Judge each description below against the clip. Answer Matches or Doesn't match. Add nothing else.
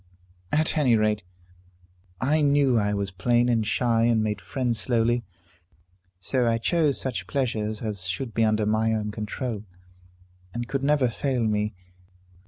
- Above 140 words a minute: Matches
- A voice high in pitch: Doesn't match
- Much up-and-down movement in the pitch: Doesn't match